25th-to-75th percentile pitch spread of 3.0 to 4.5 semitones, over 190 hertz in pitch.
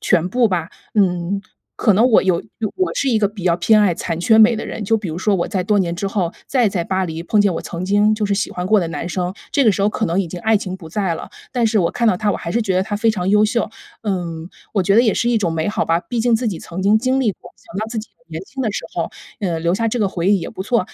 Yes: average, 3.6 semitones; high, 200 Hz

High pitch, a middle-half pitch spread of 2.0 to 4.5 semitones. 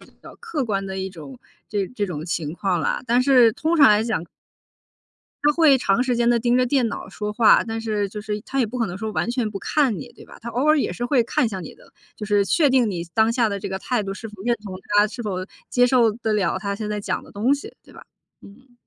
Yes: high, 220 Hz; average, 3.7 semitones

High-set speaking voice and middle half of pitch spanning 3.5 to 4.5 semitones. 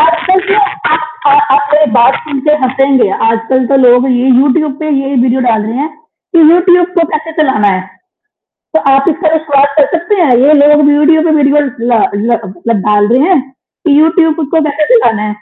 Yes: very high, 285 Hz; average, 4.2 semitones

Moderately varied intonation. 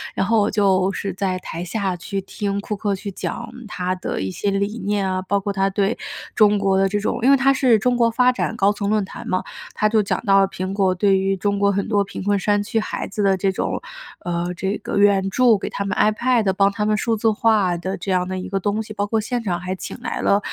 No: narrow, 1.8 semitones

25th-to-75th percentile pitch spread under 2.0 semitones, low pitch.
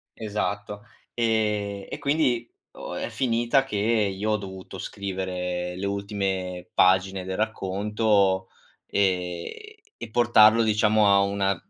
No: narrow, 2.5 semitones; low, 100 Hz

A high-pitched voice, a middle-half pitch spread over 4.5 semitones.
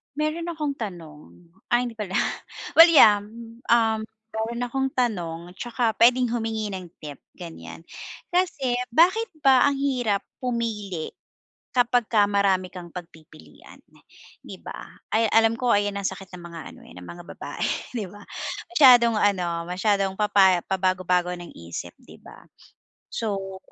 Yes: high, 210 Hz; average, 4.9 semitones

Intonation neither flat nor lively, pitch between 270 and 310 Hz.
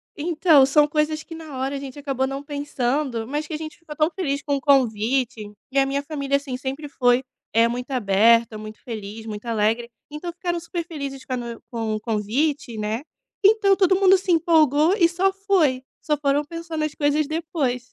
Yes: average, 4.4 semitones; very high, 280 Hz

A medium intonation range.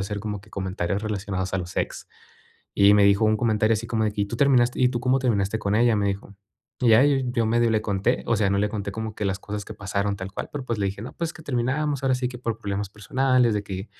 Yes: average, 3.2 semitones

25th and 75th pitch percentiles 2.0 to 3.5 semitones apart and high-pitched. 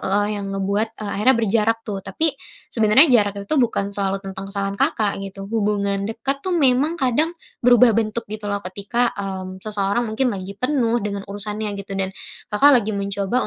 Yes: average, 3.1 semitones; high, 210 Hz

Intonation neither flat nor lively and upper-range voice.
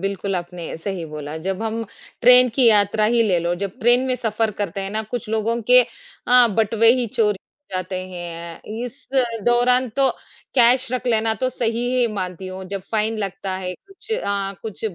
Yes: average, 4.1 semitones; high, 215 Hz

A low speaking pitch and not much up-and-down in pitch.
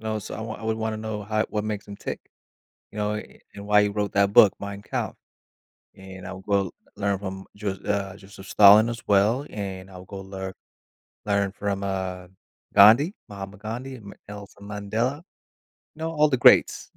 Yes: low, 100 Hz; narrow, 1.8 semitones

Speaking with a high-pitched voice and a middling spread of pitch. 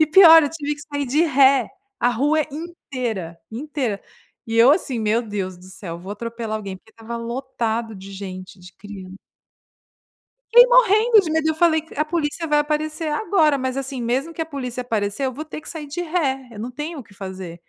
No: very high, 265 Hz; wide, 6.1 semitones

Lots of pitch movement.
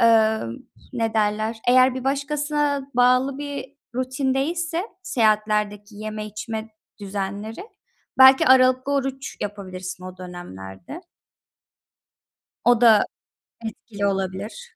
No: average, 4.5 semitones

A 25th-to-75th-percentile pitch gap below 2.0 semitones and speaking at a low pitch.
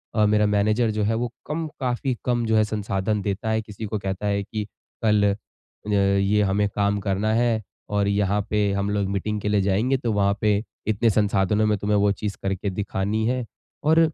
Yes: narrow, 1.6 semitones; low, 105 Hz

